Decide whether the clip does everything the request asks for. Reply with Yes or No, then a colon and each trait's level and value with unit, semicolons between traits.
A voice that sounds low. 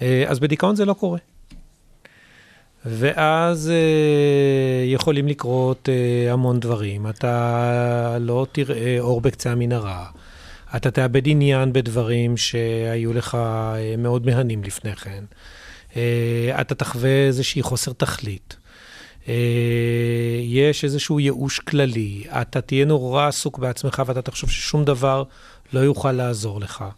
Yes: low, 125 Hz